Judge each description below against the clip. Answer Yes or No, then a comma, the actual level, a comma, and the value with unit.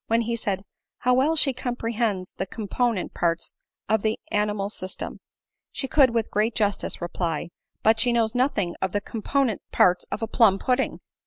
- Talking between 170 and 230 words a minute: Yes, average, 180 wpm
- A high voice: Yes, high, 220 Hz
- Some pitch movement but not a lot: Yes, average, 3.7 semitones